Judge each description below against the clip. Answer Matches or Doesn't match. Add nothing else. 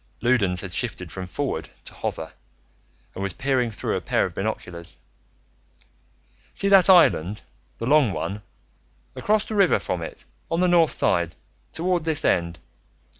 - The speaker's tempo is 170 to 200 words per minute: Doesn't match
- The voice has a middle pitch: Doesn't match